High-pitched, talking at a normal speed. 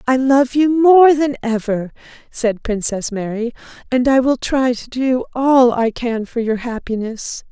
Yes: high, 245 Hz; average, 170 wpm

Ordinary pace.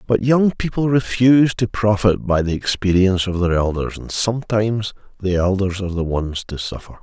Yes: average, 180 wpm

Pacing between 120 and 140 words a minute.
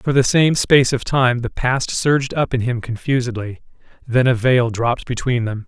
No: average, 200 wpm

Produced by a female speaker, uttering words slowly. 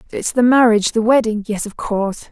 No: female; fast, 210 wpm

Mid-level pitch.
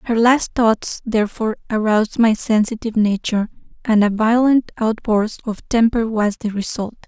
No: high, 220 Hz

